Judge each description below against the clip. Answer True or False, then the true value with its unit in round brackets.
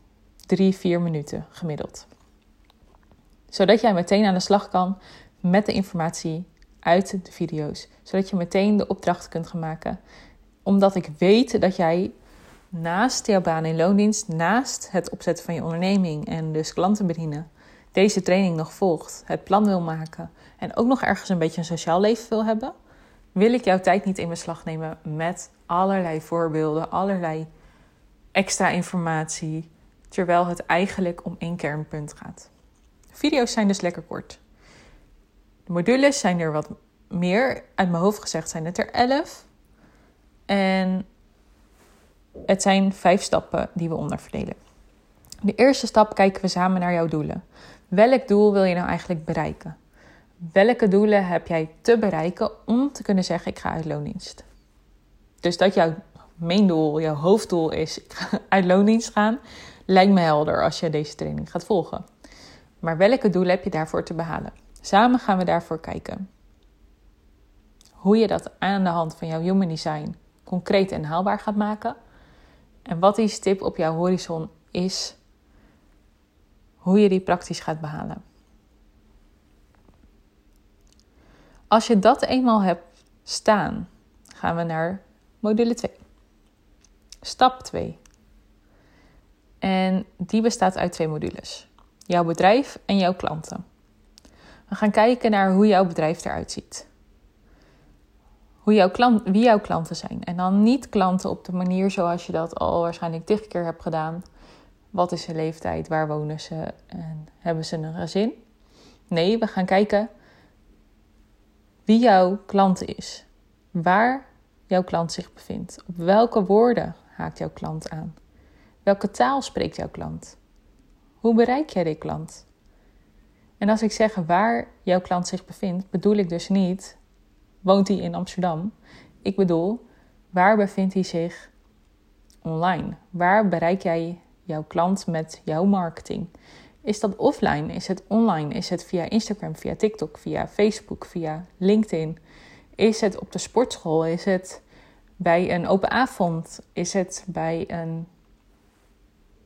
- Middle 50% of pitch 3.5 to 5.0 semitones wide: True (4.0 semitones)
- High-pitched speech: False (180 Hz)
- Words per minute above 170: False (150 wpm)